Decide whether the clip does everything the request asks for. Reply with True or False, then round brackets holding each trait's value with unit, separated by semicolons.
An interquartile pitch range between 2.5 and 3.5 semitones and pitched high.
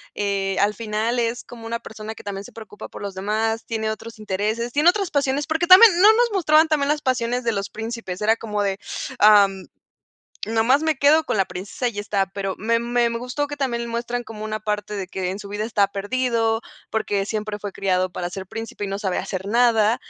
True (3.2 semitones; 225 Hz)